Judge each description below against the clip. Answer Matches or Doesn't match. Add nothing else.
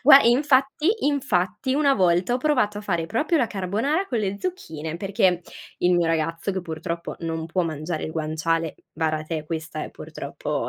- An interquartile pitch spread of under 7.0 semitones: Doesn't match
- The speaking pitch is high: Doesn't match